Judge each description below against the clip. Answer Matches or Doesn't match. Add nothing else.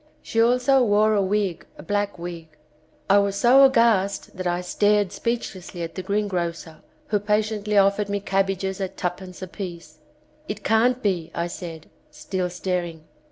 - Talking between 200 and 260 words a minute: Doesn't match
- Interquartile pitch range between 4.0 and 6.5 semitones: Doesn't match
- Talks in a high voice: Matches